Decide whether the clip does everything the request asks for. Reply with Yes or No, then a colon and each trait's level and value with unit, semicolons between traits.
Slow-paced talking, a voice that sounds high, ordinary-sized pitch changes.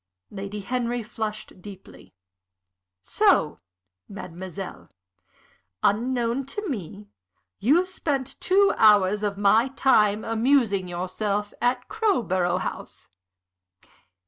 Yes: slow, 90 wpm; high, 215 Hz; average, 4.6 semitones